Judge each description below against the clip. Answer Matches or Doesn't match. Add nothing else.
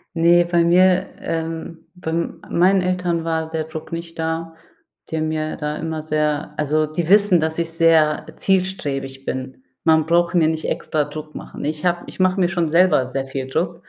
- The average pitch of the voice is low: Doesn't match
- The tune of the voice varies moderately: Doesn't match